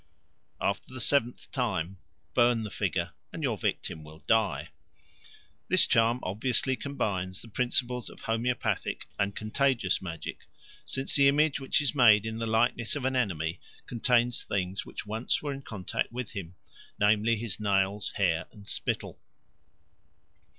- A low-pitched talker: Yes, low, 115 Hz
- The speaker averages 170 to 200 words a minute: No, average, 145 wpm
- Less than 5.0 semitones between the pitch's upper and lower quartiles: Yes, average, 4.0 semitones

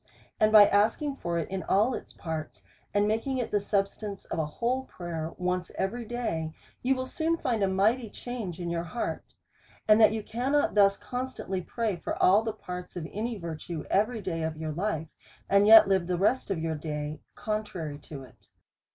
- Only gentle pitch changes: No, average, 4.9 semitones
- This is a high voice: Yes, high, 200 Hz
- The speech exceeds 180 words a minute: Yes, average, 195 wpm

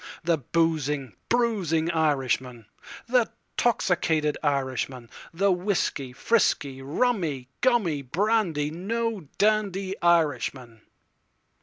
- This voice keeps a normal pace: No, slow, 70 wpm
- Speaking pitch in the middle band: Yes, medium, 165 Hz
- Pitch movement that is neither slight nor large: No, wide, 6.6 semitones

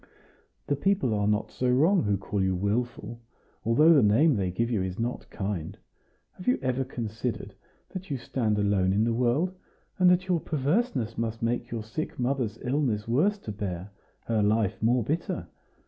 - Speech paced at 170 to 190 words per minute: Yes, average, 180 wpm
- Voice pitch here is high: No, low, 115 Hz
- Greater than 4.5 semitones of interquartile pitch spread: Yes, average, 5.1 semitones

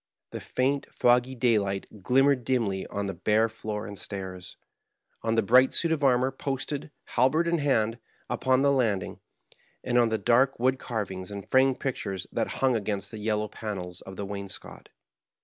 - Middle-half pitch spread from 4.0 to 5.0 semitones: Yes, average, 4.5 semitones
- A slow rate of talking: No, average, 165 wpm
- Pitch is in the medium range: No, low, 115 Hz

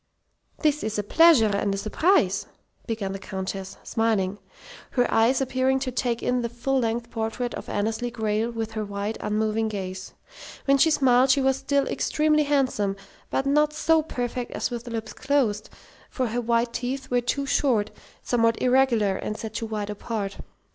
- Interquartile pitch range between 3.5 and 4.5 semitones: Yes, average, 3.8 semitones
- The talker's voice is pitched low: No, high, 235 Hz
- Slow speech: No, average, 170 wpm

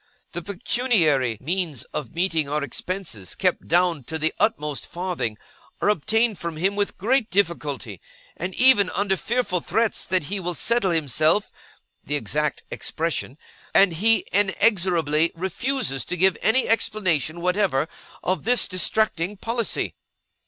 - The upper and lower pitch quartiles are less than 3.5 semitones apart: No, average, 4.8 semitones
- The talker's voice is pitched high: No, medium, 180 Hz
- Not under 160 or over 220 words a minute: No, slow, 135 wpm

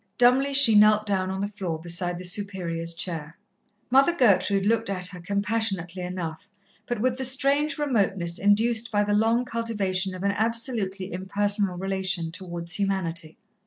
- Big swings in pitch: No, average, 3.9 semitones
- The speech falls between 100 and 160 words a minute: Yes, average, 155 wpm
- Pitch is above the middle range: Yes, high, 200 Hz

